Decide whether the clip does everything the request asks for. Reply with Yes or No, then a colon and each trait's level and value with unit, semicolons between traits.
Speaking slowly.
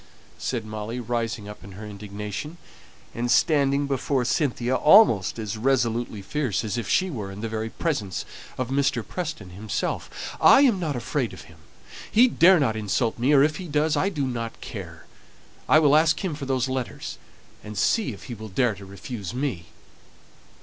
No: average, 175 wpm